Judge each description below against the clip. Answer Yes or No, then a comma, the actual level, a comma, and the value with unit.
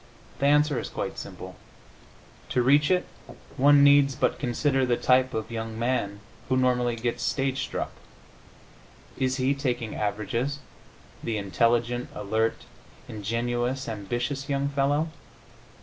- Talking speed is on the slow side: Yes, slow, 125 wpm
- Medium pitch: No, low, 125 Hz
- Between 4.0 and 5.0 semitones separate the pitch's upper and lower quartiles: No, average, 3.0 semitones